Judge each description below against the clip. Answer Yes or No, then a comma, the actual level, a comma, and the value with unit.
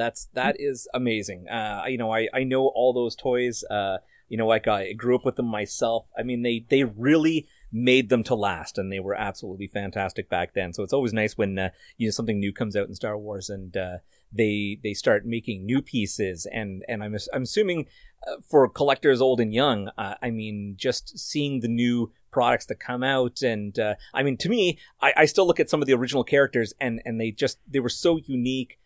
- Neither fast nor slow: No, fast, 220 wpm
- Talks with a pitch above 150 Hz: No, low, 115 Hz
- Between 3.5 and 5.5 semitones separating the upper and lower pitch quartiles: Yes, average, 3.8 semitones